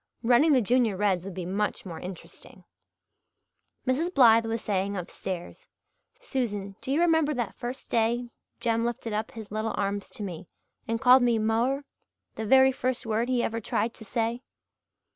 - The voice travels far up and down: No, average, 3.5 semitones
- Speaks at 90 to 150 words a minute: No, average, 165 wpm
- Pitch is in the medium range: No, high, 230 Hz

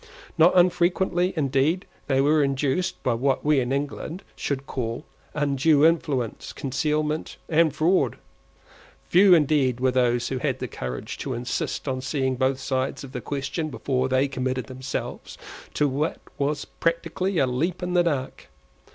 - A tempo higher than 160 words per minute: No, average, 150 wpm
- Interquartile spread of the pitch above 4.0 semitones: No, average, 3.6 semitones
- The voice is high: No, medium, 140 Hz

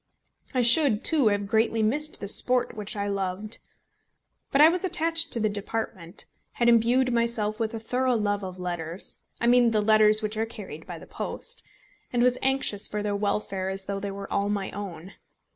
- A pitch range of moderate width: Yes, average, 3.2 semitones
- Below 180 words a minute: No, average, 195 wpm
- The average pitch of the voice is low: No, high, 215 Hz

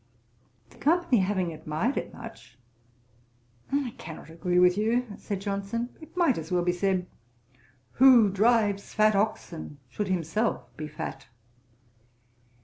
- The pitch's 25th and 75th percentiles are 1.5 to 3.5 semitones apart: No, average, 4.8 semitones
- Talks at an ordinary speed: No, slow, 130 wpm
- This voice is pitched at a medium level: No, high, 200 Hz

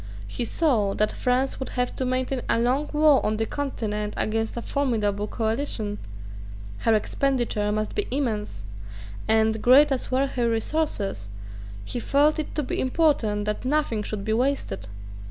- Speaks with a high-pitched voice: Yes, high, 240 Hz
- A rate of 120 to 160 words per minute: Yes, average, 155 wpm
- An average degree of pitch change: Yes, average, 4.4 semitones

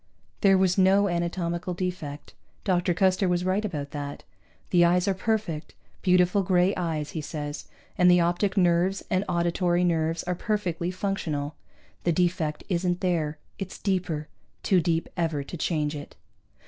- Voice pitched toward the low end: No, medium, 175 Hz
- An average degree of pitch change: No, narrow, 2.3 semitones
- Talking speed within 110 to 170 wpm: Yes, average, 150 wpm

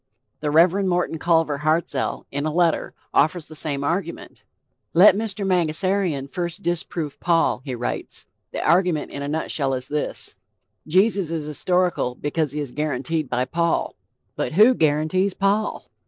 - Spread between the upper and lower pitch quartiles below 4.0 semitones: Yes, average, 3.5 semitones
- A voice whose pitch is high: No, medium, 160 Hz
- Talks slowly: No, average, 150 wpm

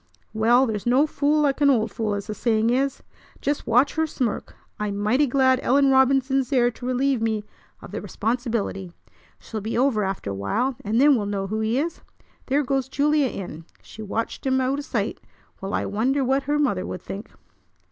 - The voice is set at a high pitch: Yes, high, 245 Hz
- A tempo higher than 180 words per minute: Yes, average, 200 wpm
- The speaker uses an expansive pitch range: No, average, 4.1 semitones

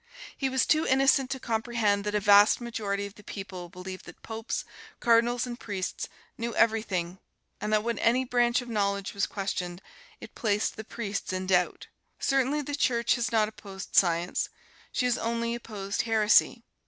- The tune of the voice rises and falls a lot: No, average, 3.1 semitones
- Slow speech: No, average, 170 wpm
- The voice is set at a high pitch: Yes, high, 220 Hz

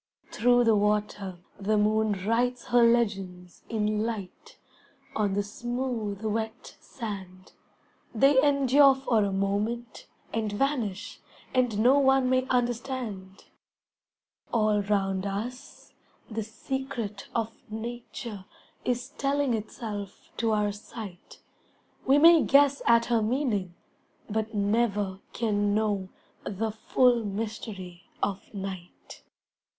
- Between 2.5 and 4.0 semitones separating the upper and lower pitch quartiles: Yes, average, 3.2 semitones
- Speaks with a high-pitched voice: Yes, high, 220 Hz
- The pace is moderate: No, slow, 110 wpm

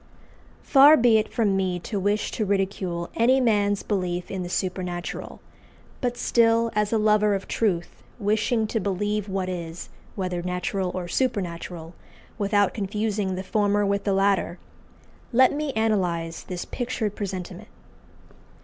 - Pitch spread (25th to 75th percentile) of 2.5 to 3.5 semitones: Yes, average, 3.0 semitones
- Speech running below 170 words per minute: Yes, average, 140 wpm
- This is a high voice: Yes, high, 200 Hz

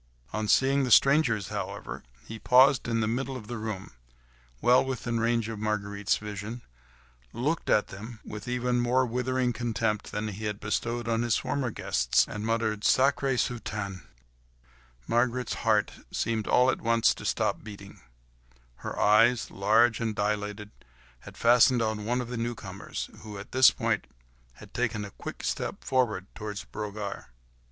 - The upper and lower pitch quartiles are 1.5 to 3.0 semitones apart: Yes, narrow, 2.6 semitones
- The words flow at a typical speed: Yes, average, 155 wpm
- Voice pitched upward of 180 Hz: No, low, 115 Hz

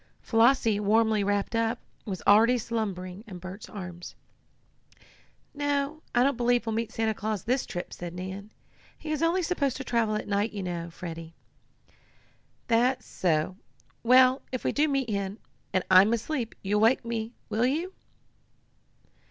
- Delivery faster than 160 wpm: No, average, 155 wpm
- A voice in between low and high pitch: No, high, 225 Hz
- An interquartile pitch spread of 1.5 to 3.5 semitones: No, average, 4.4 semitones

